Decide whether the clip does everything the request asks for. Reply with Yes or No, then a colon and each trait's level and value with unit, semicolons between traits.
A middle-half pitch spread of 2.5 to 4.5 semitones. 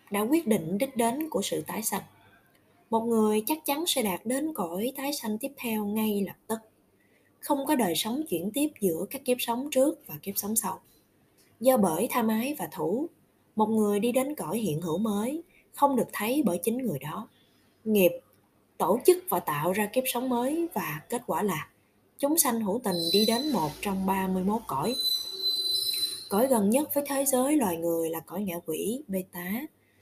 No: wide, 5.4 semitones